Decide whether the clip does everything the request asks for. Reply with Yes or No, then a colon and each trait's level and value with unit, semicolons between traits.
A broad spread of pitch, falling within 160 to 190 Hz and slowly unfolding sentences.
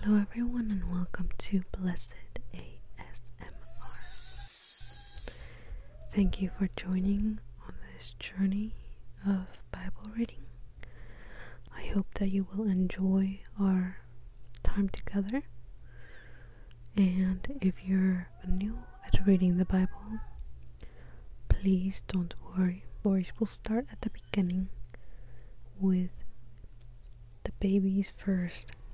Yes: wide, 8.7 semitones; medium, 185 Hz; slow, 95 wpm